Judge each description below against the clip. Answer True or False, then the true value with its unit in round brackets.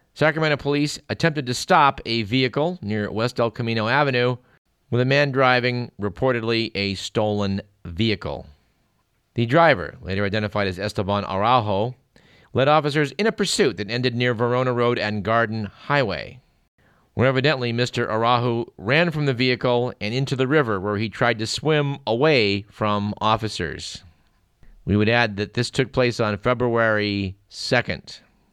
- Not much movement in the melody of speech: False (3.9 semitones)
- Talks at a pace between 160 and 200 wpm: False (145 wpm)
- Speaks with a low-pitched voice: True (120 Hz)